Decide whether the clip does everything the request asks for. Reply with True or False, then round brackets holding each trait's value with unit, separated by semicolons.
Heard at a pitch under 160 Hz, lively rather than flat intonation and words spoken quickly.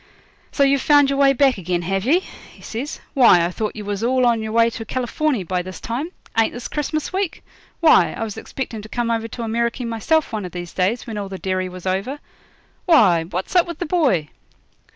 False (230 Hz; 6.2 semitones; 220 wpm)